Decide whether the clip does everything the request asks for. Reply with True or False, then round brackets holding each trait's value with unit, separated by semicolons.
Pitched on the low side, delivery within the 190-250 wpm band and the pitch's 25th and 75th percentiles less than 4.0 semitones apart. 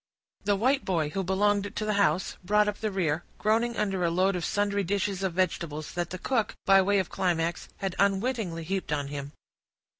False (195 Hz; 200 wpm; 3.1 semitones)